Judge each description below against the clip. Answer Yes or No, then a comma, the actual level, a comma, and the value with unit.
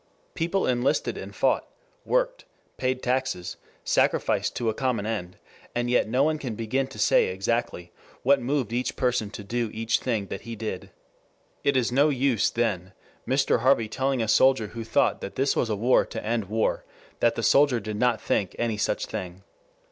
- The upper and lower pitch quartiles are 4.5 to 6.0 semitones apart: No, average, 3.4 semitones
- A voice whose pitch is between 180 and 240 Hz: No, low, 120 Hz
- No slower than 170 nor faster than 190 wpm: Yes, average, 180 wpm